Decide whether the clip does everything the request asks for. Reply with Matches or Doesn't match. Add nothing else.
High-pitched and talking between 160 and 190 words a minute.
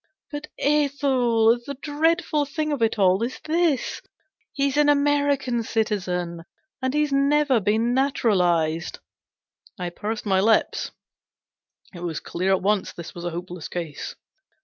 Doesn't match